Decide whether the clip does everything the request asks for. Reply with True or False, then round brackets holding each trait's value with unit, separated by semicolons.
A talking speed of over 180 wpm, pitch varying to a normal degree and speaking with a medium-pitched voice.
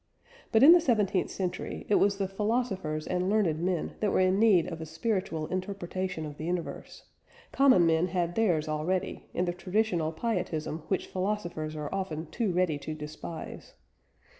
False (165 wpm; 3.9 semitones; 180 Hz)